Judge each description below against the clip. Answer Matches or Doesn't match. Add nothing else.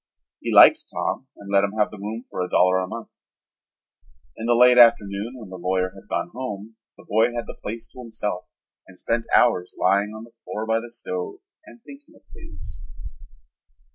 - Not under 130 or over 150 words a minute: Doesn't match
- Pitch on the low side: Matches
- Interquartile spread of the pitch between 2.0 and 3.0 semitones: Doesn't match